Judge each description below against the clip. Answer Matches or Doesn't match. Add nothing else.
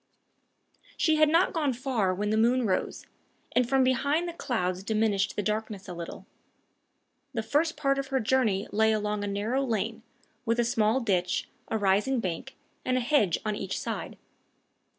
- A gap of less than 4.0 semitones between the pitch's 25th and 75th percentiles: Doesn't match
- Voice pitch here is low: Doesn't match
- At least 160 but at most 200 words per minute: Matches